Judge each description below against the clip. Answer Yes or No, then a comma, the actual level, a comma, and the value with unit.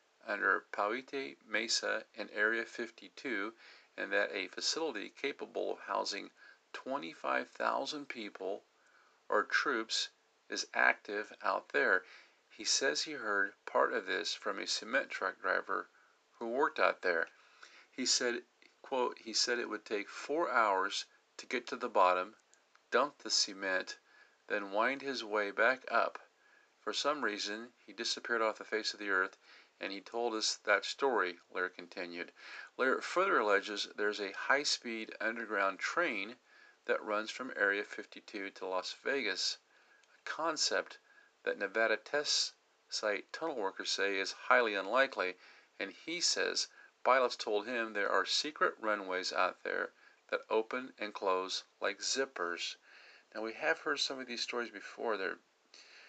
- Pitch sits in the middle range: Yes, medium, 150 Hz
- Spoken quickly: No, average, 145 wpm